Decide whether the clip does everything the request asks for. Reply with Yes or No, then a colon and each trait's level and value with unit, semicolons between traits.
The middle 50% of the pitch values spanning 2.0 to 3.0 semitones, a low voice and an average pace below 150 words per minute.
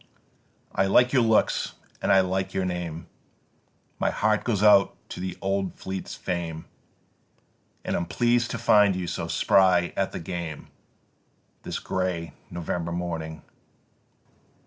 Yes: narrow, 2.4 semitones; very low, 95 Hz; average, 140 wpm